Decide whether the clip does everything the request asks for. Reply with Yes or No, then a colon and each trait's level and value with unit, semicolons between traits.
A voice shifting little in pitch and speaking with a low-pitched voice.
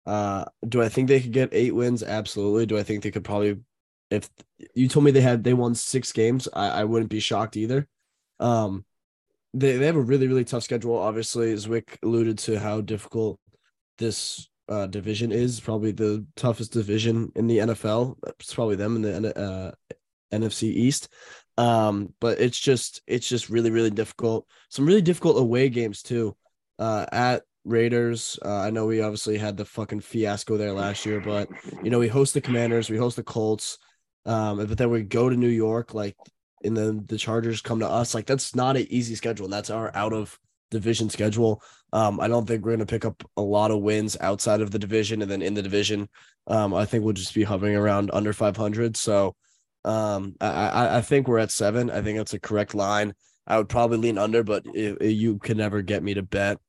Yes: narrow, 2.1 semitones; low, 110 Hz